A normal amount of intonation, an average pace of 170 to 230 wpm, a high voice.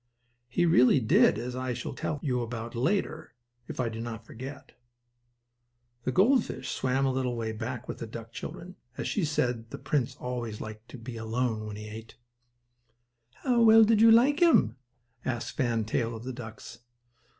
No: average, 4.1 semitones; average, 185 wpm; low, 125 Hz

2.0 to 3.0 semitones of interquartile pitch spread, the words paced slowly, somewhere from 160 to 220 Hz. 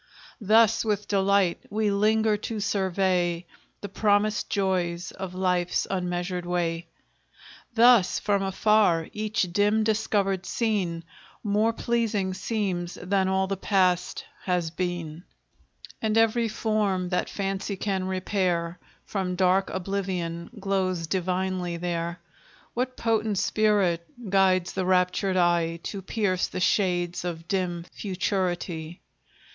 Yes: average, 2.7 semitones; slow, 115 wpm; high, 190 Hz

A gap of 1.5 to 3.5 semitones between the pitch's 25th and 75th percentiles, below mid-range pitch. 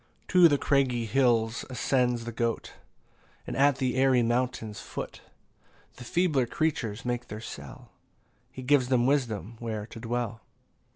Yes: narrow, 2.6 semitones; low, 120 Hz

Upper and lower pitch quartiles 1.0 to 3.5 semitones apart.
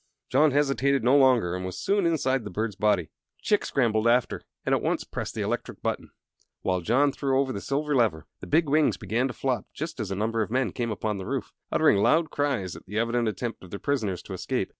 No: average, 4.9 semitones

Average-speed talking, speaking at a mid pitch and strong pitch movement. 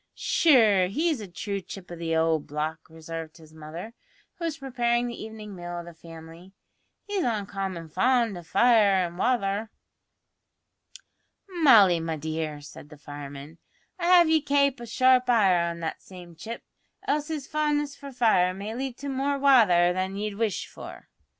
No: average, 165 wpm; high, 200 Hz; wide, 7.4 semitones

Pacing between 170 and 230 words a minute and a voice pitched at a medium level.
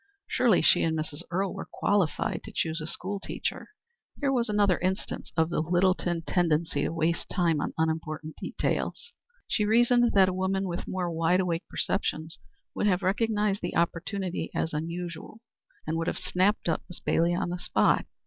Yes: average, 175 wpm; medium, 175 Hz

